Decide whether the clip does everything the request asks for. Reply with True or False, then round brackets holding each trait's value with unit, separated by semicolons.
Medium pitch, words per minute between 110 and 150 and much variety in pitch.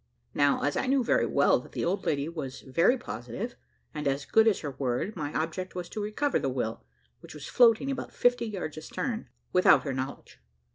False (165 Hz; 200 wpm; 8.0 semitones)